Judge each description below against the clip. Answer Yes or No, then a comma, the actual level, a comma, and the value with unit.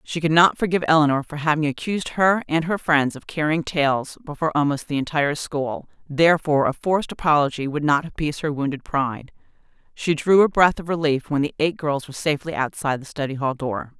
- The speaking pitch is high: No, medium, 150 Hz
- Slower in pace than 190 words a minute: No, average, 200 wpm